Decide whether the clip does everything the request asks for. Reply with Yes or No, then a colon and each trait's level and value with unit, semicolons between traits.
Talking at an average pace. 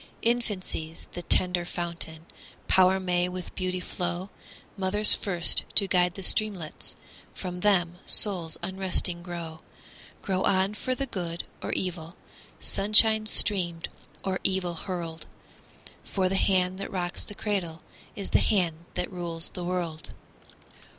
No: slow, 130 wpm